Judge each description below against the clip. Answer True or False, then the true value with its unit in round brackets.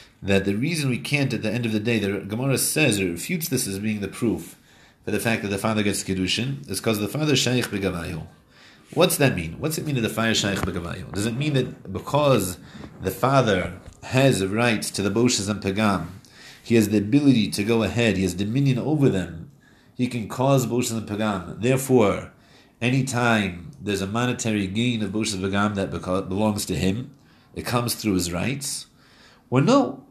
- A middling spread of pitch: True (4.2 semitones)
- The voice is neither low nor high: False (110 Hz)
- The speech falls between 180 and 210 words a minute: True (200 wpm)